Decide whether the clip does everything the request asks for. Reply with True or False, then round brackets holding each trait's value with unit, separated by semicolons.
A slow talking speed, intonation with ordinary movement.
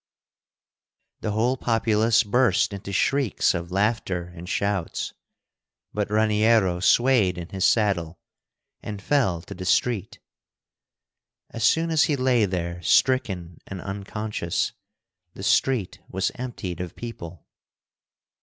True (115 wpm; 4.5 semitones)